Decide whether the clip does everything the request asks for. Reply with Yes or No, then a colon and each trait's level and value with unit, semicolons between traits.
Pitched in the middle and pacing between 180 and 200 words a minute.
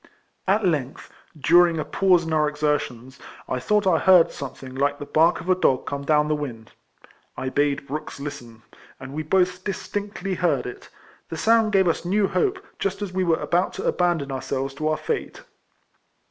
Yes: medium, 160 Hz; average, 190 wpm